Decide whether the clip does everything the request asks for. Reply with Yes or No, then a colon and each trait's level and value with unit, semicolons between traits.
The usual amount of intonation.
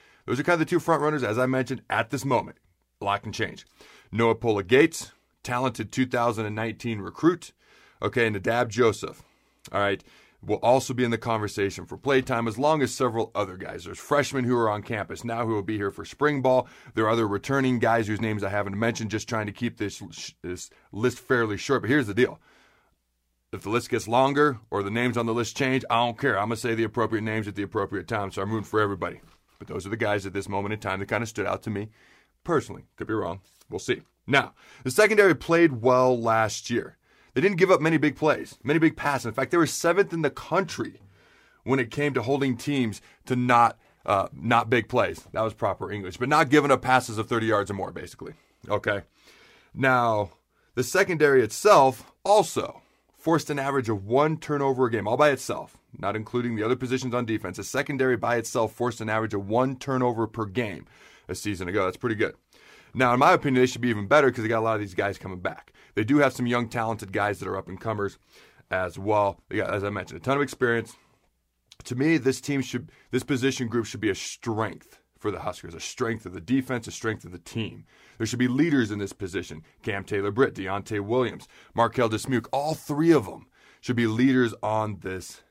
Yes: average, 3.8 semitones